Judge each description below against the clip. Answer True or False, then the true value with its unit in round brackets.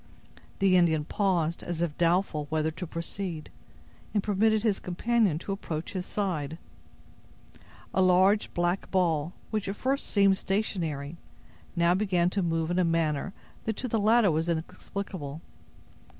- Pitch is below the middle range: False (180 Hz)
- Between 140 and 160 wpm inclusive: True (145 wpm)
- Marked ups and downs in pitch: False (3.5 semitones)